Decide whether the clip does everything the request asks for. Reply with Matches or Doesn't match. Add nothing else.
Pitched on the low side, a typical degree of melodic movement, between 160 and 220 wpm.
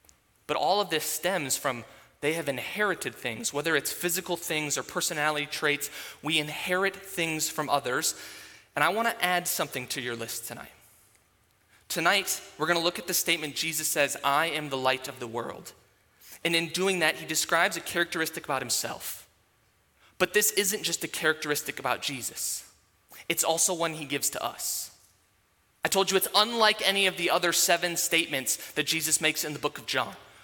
Doesn't match